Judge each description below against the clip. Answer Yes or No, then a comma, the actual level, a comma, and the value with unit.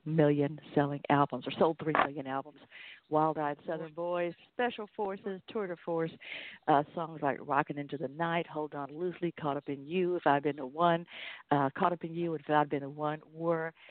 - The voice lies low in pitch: No, medium, 155 Hz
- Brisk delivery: Yes, fast, 210 wpm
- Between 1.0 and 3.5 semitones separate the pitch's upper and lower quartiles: Yes, average, 3.0 semitones